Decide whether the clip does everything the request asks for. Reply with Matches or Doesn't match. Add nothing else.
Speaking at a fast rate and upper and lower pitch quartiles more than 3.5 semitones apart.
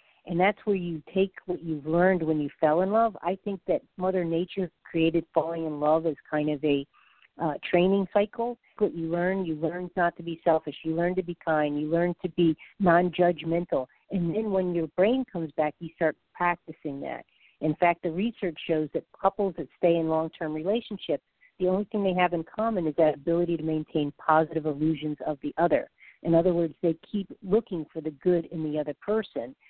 Doesn't match